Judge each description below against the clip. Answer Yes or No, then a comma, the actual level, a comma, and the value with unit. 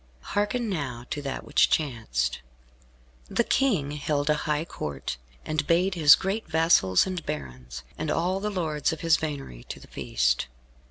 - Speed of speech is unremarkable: Yes, average, 160 wpm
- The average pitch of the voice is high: No, medium, 150 Hz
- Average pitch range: No, wide, 6.8 semitones